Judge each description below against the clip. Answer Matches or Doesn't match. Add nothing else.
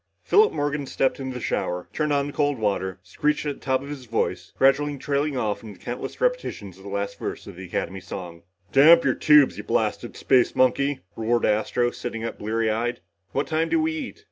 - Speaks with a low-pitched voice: Matches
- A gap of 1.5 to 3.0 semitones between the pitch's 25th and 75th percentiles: Doesn't match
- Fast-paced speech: Matches